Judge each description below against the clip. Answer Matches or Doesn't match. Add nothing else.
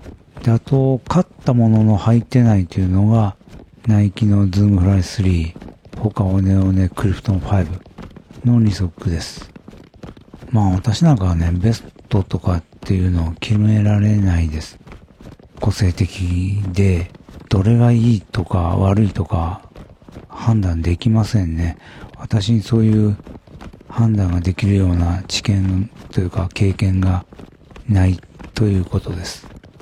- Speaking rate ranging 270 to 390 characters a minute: Doesn't match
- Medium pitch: Doesn't match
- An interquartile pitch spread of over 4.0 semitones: Doesn't match